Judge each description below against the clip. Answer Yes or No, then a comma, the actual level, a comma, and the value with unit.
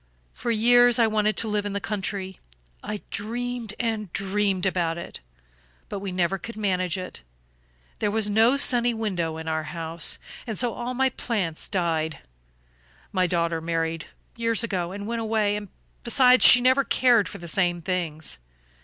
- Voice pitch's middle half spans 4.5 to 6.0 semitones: Yes, average, 4.8 semitones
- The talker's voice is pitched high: Yes, high, 205 Hz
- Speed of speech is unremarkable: Yes, average, 160 wpm